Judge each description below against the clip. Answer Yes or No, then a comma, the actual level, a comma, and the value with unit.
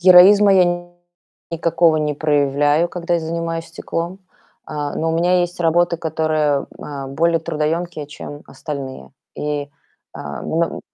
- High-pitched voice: No, medium, 165 Hz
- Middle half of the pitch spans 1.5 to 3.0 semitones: Yes, narrow, 2.6 semitones